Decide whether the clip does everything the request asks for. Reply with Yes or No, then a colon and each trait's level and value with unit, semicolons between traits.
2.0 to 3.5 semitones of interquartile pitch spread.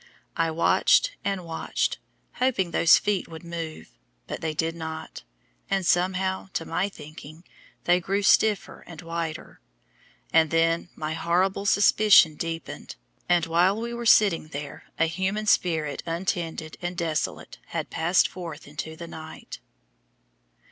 Yes: average, 2.8 semitones